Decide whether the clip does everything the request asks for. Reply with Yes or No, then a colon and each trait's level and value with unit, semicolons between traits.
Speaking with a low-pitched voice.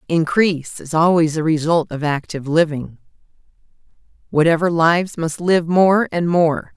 No: medium, 165 Hz